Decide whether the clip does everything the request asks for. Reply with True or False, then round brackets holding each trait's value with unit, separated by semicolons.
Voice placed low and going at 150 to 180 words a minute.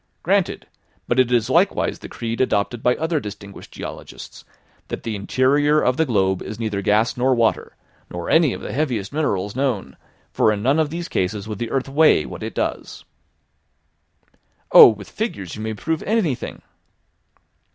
True (120 Hz; 170 wpm)